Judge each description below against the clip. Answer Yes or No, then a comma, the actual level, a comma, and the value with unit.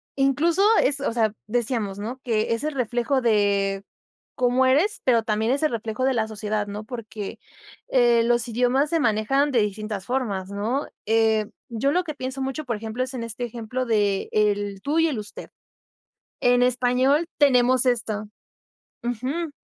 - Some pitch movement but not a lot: Yes, average, 3.4 semitones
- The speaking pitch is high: Yes, high, 240 Hz